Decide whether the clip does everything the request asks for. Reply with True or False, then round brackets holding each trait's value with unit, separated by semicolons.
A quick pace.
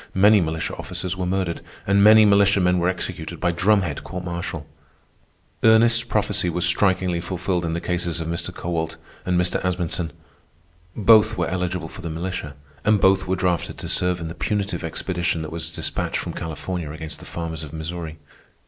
False (175 wpm)